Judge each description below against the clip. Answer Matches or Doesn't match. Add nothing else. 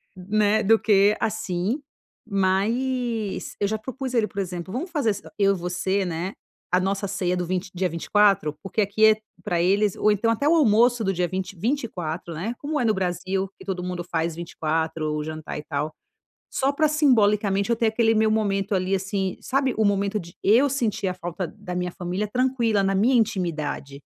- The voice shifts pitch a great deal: Doesn't match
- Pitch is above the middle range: Matches